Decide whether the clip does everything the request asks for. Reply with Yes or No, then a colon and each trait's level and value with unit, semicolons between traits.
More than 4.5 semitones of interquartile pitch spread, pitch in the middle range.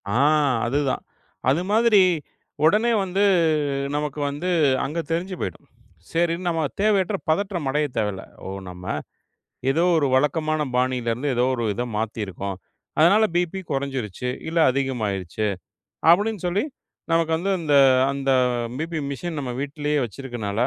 Yes: wide, 5.6 semitones; medium, 150 Hz